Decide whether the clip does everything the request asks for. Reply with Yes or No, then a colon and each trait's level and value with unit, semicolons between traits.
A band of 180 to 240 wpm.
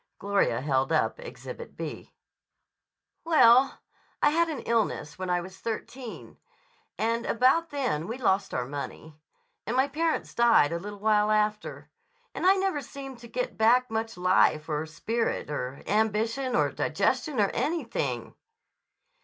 No: average, 145 wpm